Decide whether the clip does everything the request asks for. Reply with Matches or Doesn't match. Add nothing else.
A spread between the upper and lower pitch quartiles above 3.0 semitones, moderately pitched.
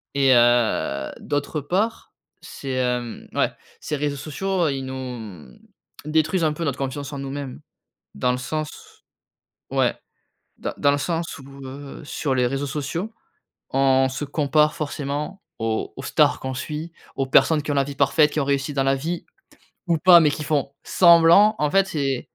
Doesn't match